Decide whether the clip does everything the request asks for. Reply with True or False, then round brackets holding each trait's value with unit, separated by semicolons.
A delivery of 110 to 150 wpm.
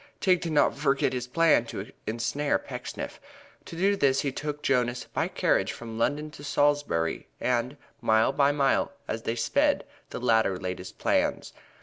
False (170 wpm)